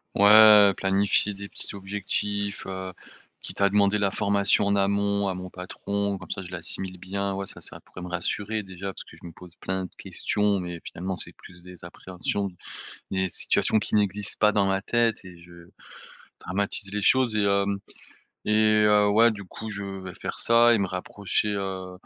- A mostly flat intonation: Yes, narrow, 1.6 semitones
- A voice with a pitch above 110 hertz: No, low, 100 Hz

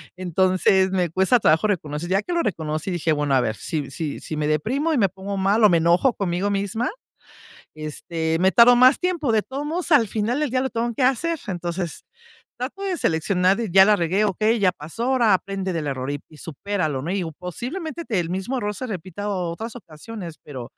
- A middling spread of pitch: No, wide, 5.9 semitones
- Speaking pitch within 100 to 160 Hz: No, high, 190 Hz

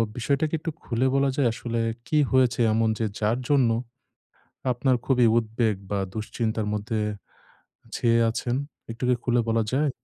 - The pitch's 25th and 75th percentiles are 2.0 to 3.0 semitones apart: Yes, narrow, 2.6 semitones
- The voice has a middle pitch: No, low, 120 Hz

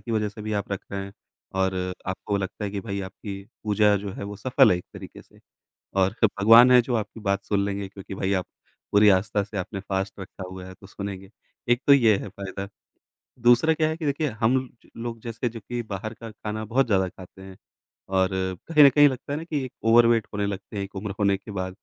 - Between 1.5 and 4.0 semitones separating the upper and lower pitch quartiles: Yes, average, 3.2 semitones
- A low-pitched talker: Yes, low, 105 Hz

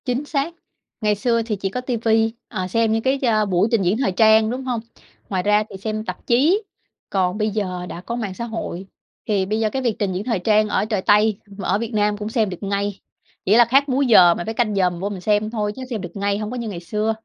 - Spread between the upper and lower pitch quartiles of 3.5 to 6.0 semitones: No, average, 2.8 semitones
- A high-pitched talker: Yes, high, 215 Hz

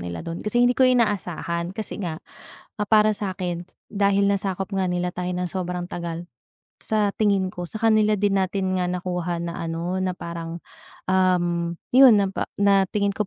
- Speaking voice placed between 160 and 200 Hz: Yes, medium, 185 Hz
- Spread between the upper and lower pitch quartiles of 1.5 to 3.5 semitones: Yes, narrow, 2.6 semitones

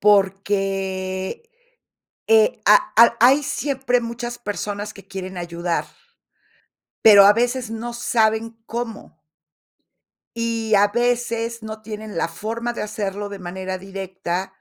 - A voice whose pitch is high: Yes, high, 215 Hz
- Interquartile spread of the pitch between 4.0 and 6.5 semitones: No, average, 3.3 semitones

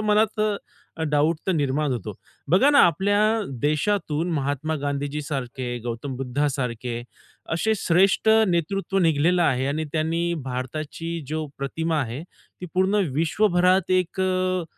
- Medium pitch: Yes, medium, 160 Hz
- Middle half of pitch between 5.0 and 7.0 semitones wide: No, average, 4.6 semitones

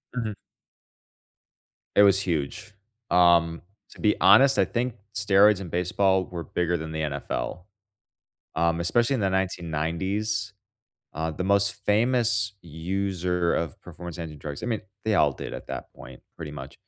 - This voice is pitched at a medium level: No, very low, 90 Hz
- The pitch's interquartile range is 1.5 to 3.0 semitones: No, average, 3.6 semitones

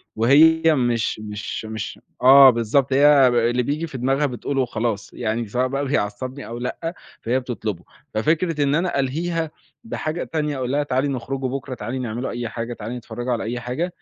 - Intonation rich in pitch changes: No, average, 3.4 semitones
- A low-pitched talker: Yes, low, 130 Hz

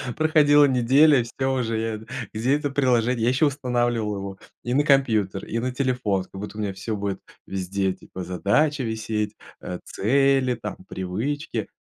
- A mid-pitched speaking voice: No, low, 115 Hz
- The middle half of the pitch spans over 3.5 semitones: Yes, average, 4.7 semitones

